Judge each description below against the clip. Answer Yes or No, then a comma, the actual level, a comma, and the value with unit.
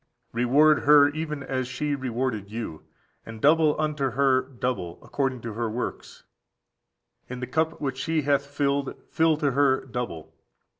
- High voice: No, low, 135 Hz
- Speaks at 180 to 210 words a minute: No, average, 155 wpm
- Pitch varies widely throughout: No, average, 3.1 semitones